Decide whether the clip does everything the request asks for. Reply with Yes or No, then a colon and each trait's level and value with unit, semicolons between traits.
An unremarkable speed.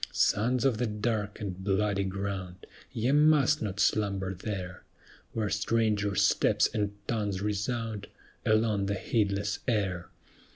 No: slow, 125 wpm